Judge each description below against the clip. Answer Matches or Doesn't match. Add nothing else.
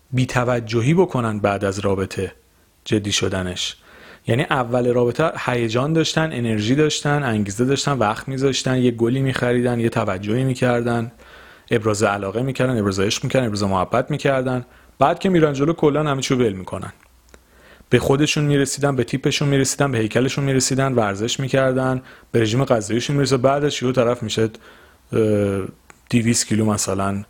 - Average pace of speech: Matches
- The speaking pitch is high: Doesn't match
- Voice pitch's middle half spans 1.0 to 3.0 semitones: Doesn't match